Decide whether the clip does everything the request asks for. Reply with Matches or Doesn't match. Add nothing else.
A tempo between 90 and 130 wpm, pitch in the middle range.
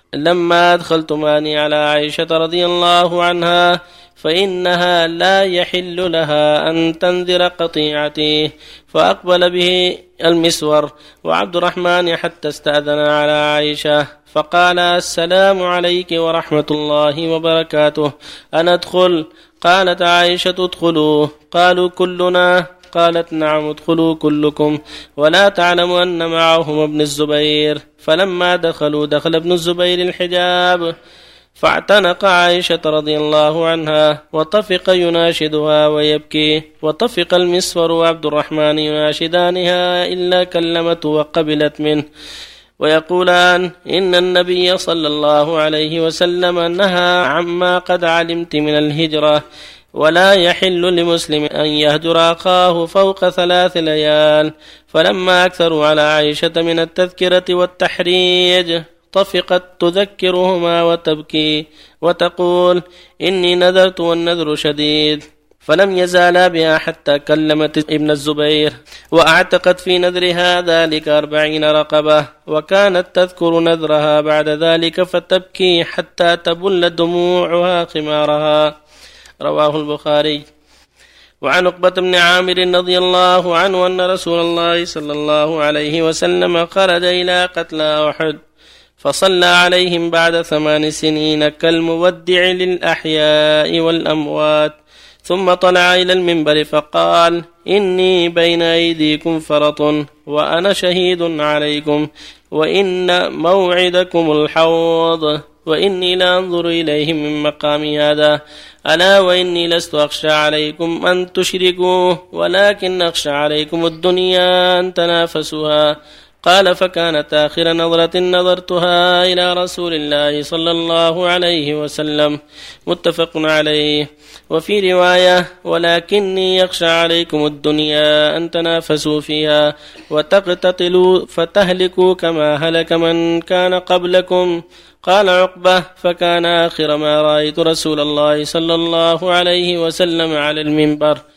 Matches